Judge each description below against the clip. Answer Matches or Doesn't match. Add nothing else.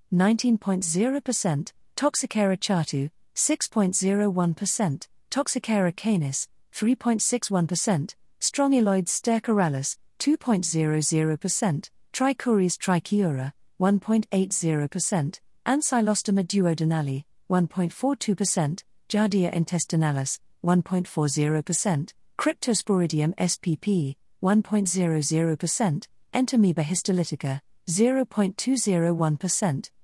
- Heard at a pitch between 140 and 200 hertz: Matches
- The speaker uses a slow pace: Matches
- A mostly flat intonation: Doesn't match